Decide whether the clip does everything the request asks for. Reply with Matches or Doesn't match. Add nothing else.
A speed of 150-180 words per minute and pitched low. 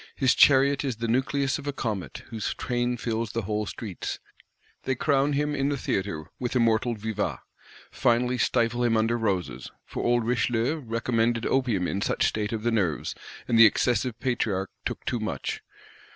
Matches